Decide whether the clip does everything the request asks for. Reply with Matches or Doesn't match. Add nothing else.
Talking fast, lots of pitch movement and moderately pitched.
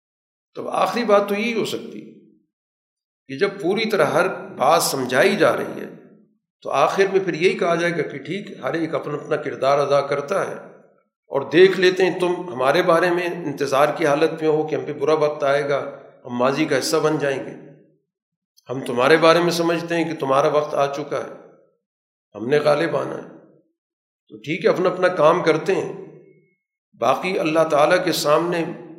Doesn't match